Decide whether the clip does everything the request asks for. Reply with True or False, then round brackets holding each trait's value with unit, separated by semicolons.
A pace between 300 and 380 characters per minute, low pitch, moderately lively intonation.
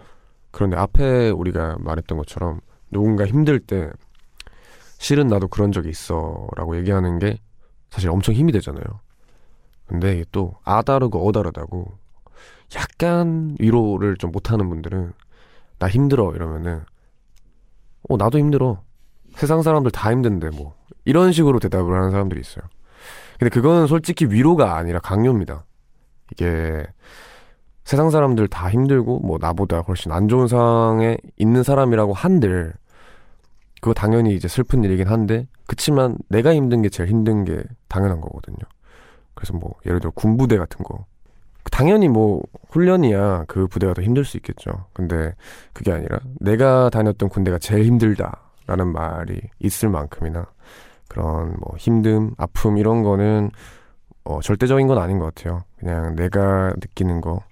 True (305 characters per minute; 105 Hz; 5.0 semitones)